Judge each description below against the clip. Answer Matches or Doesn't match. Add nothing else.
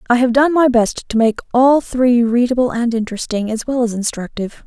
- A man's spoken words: Doesn't match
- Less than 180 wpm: Doesn't match